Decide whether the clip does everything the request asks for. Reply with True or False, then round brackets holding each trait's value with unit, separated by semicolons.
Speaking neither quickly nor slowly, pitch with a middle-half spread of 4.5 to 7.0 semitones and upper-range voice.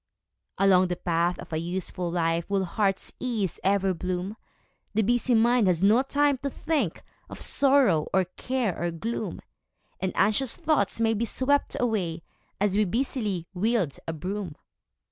True (155 wpm; 5.1 semitones; 200 Hz)